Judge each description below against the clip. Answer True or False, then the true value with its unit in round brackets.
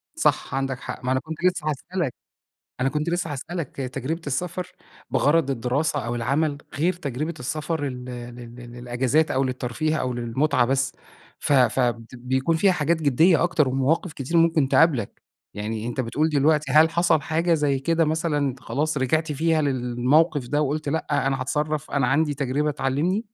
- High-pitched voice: False (145 Hz)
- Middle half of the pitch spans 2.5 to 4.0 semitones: True (3.7 semitones)